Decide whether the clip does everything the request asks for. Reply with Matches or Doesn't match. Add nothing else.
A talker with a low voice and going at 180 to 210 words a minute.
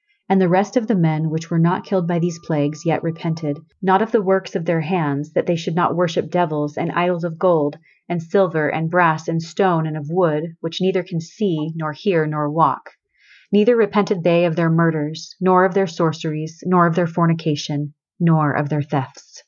Doesn't match